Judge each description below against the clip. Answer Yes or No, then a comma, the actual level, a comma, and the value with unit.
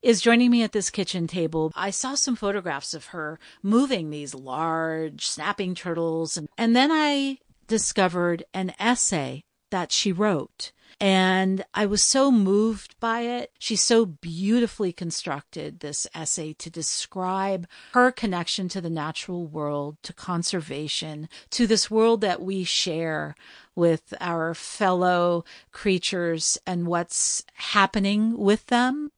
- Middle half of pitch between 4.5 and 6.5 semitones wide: Yes, average, 4.9 semitones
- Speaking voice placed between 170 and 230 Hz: Yes, medium, 185 Hz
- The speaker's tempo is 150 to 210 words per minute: No, slow, 135 wpm